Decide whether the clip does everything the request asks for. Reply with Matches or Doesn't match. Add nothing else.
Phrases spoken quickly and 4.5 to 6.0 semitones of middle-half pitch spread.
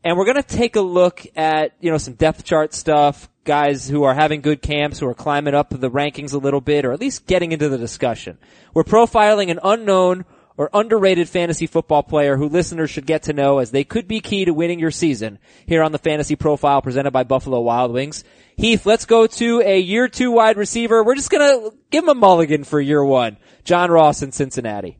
Matches